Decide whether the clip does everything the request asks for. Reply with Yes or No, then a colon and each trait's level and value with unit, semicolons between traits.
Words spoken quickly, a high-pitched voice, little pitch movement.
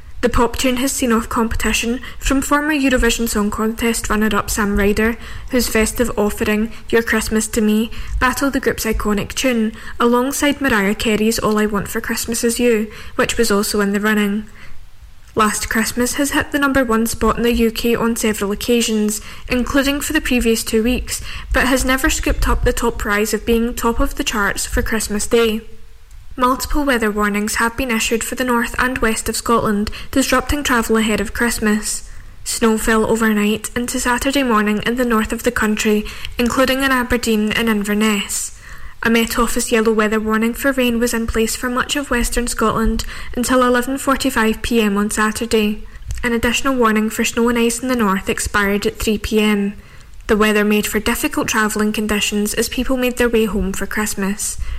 No: average, 180 wpm; high, 230 Hz; narrow, 2.3 semitones